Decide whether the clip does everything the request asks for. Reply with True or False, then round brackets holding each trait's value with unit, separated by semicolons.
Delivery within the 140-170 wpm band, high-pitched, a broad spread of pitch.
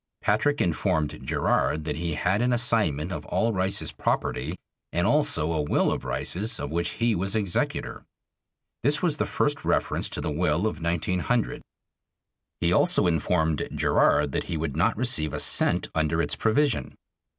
False (160 wpm; 90 Hz; 6.4 semitones)